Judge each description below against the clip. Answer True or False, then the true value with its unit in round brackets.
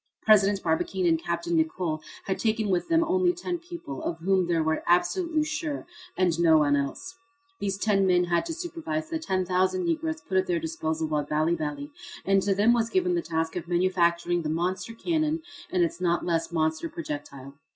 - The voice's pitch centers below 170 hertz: False (180 Hz)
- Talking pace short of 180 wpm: False (190 wpm)